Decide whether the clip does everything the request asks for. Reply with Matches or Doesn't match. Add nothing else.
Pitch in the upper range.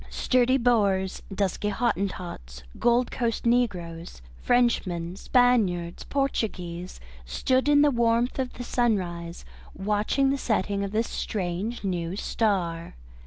Matches